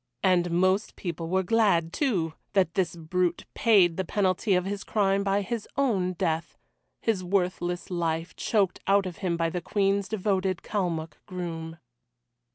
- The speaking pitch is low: No, medium, 185 Hz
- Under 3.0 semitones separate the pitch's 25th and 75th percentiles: Yes, narrow, 2.5 semitones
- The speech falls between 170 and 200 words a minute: No, average, 155 wpm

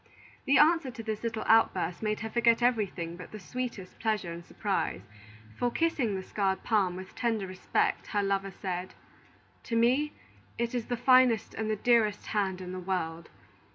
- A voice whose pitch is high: Yes, high, 215 Hz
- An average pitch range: Yes, average, 4.0 semitones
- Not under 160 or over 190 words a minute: Yes, average, 175 wpm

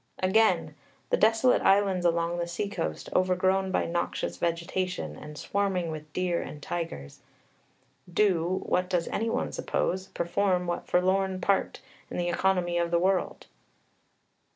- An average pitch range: No, narrow, 2.0 semitones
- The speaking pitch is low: No, medium, 180 Hz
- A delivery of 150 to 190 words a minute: No, average, 140 wpm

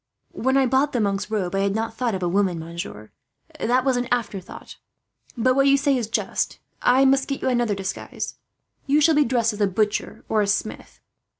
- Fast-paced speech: Yes, fast, 210 wpm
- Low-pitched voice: No, high, 230 Hz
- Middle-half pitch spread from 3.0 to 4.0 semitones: No, average, 4.8 semitones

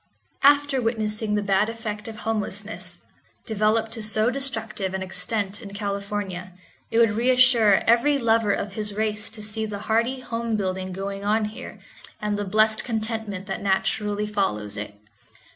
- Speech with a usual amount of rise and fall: No, narrow, 2.1 semitones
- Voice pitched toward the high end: Yes, high, 215 Hz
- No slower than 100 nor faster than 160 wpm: Yes, average, 155 wpm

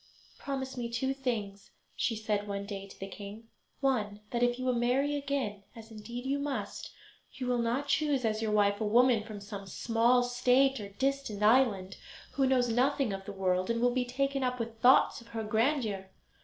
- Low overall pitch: No, high, 235 Hz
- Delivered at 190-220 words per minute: Yes, average, 195 wpm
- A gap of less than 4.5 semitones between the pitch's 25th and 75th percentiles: Yes, average, 3.8 semitones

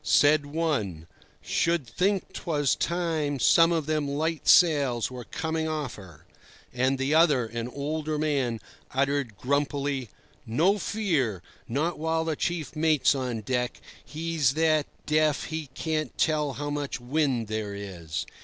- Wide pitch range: No, average, 4.0 semitones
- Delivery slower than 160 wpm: Yes, average, 140 wpm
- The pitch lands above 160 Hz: No, medium, 145 Hz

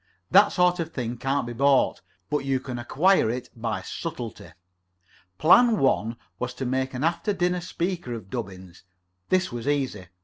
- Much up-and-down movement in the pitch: Yes, wide, 6.2 semitones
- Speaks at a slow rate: No, average, 170 wpm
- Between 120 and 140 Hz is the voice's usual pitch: Yes, low, 135 Hz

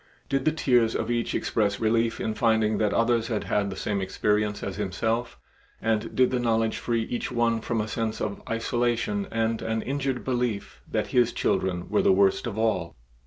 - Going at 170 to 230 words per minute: Yes, average, 190 wpm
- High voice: No, low, 115 Hz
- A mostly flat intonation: Yes, narrow, 2.1 semitones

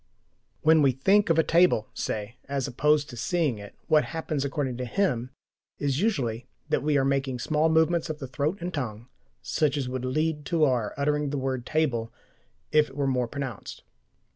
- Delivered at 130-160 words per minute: No, average, 190 wpm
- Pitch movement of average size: Yes, average, 3.6 semitones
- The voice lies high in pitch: No, medium, 140 Hz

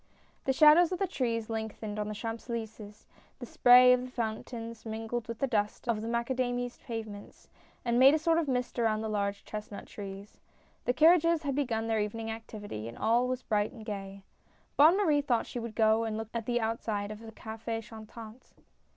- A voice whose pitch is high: Yes, high, 225 Hz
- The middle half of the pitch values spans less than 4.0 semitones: Yes, narrow, 2.5 semitones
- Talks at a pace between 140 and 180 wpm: No, average, 200 wpm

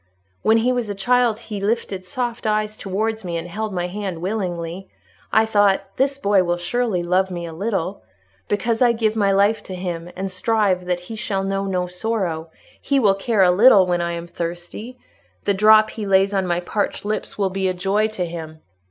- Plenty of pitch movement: No, average, 3.4 semitones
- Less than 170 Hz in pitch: No, high, 195 Hz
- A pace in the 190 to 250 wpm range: Yes, average, 200 wpm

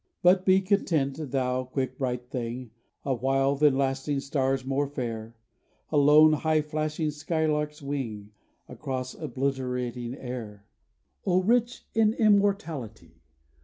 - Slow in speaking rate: Yes, slow, 120 wpm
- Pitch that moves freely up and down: No, average, 3.5 semitones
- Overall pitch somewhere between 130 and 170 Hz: Yes, medium, 140 Hz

